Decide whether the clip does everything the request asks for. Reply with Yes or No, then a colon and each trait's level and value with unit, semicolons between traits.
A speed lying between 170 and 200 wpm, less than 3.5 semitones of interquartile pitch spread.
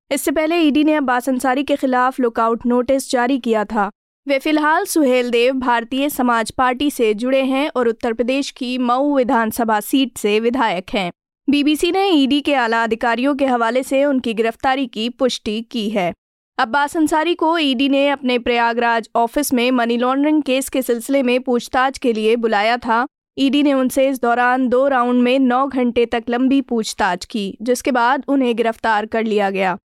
Yes: average, 180 wpm; average, 2.8 semitones